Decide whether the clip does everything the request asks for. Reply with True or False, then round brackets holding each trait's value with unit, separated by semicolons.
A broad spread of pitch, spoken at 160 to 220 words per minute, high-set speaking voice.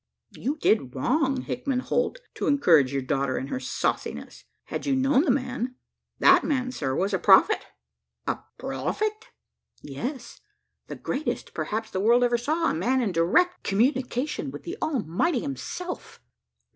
False (7.3 semitones; 150 wpm; 255 Hz)